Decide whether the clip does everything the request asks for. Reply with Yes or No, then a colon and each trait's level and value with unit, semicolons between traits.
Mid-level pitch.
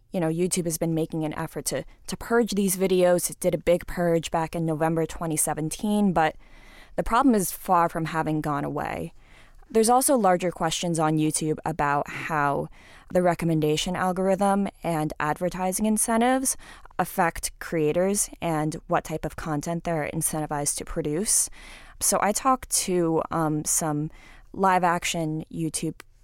Yes: medium, 165 Hz